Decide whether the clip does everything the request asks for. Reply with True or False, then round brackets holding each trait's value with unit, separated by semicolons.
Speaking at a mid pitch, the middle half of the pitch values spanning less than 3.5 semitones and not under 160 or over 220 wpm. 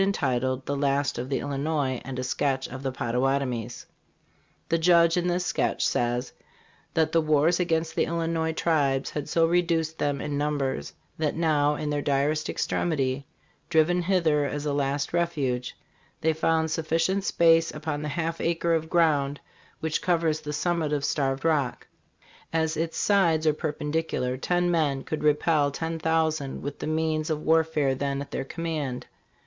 True (155 Hz; 2.8 semitones; 170 wpm)